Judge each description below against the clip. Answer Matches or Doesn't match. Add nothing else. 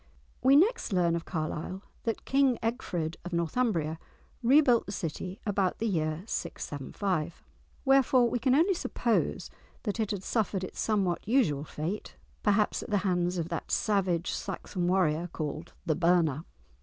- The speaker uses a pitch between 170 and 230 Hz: Matches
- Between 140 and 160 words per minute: Matches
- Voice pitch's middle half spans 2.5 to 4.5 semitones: Doesn't match